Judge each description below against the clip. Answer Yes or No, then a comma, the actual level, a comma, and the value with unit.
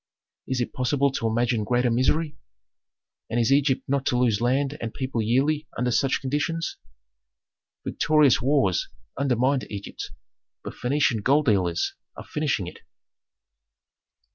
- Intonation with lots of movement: No, average, 3.4 semitones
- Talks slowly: Yes, slow, 130 wpm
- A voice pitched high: No, low, 130 Hz